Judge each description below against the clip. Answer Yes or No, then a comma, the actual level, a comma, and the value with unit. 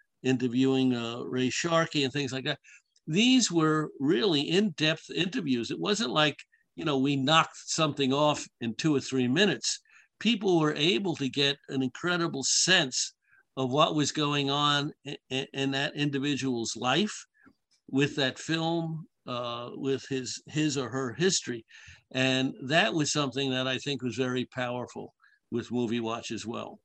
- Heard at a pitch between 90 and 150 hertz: Yes, medium, 140 Hz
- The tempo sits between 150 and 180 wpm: Yes, average, 155 wpm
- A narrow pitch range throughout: No, average, 3.4 semitones